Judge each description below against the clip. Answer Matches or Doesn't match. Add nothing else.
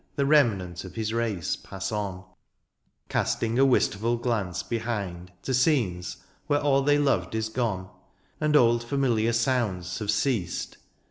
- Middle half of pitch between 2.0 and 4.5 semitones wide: Doesn't match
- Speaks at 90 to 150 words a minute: Matches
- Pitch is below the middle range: Matches